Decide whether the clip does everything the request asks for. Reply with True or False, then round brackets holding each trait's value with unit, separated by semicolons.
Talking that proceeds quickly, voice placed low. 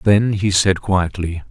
False (160 wpm; 95 Hz)